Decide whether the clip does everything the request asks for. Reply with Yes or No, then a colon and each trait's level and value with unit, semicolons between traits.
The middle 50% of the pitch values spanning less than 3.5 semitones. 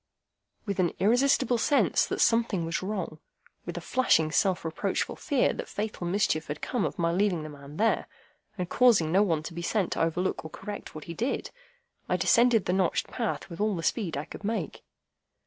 No: average, 5.3 semitones